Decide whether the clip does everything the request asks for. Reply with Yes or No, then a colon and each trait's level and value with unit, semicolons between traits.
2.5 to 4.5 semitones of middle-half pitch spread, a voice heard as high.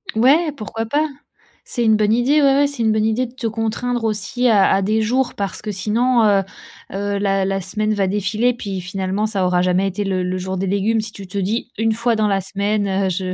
Yes: average, 2.9 semitones; high, 210 Hz